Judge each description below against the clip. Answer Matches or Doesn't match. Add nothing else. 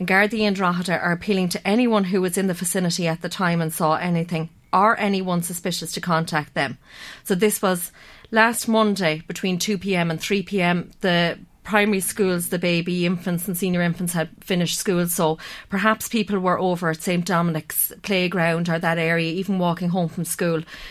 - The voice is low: Doesn't match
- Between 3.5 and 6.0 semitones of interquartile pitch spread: Doesn't match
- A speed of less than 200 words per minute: Matches